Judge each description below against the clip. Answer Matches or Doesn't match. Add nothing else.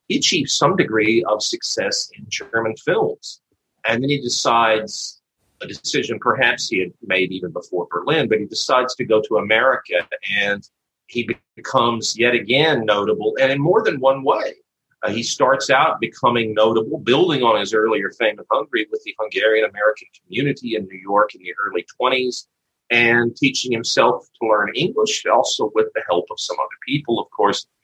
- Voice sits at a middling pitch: Doesn't match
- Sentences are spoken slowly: Doesn't match